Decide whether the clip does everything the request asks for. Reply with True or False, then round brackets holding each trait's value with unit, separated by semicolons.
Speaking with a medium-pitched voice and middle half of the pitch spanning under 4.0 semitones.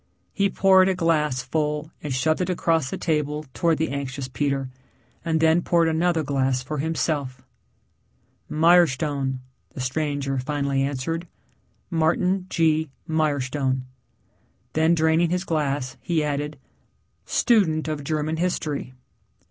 True (155 Hz; 2.9 semitones)